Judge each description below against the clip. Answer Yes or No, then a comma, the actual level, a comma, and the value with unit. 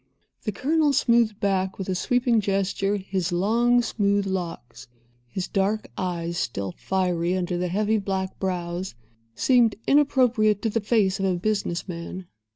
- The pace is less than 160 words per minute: Yes, average, 150 wpm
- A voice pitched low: No, high, 195 Hz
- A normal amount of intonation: Yes, average, 3.3 semitones